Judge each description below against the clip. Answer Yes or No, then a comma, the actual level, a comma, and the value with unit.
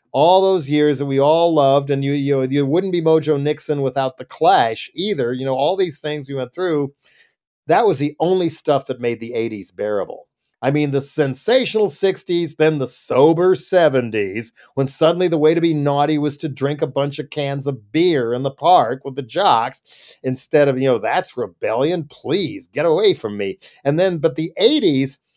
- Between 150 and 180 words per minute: No, average, 200 wpm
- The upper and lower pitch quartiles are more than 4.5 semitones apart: No, average, 3.5 semitones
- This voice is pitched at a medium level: Yes, medium, 145 Hz